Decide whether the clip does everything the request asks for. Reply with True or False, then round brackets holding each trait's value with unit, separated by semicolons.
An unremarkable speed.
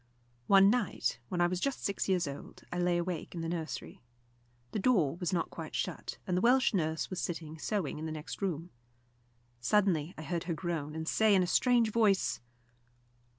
True (195 wpm)